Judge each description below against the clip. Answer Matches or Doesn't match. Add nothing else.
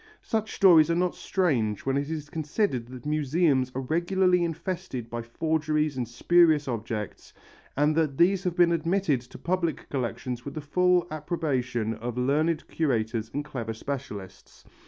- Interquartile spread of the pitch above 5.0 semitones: Matches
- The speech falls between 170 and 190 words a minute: Doesn't match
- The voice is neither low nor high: Matches